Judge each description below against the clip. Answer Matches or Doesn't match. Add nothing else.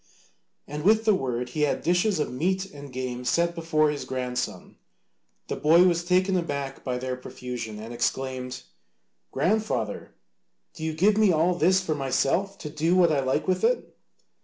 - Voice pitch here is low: Doesn't match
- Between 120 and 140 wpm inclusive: Doesn't match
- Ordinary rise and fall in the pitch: Doesn't match